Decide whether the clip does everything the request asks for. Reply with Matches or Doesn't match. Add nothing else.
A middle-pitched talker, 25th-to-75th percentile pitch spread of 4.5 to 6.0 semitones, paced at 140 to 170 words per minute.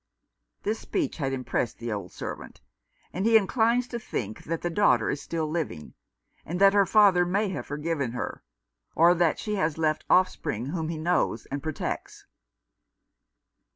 Matches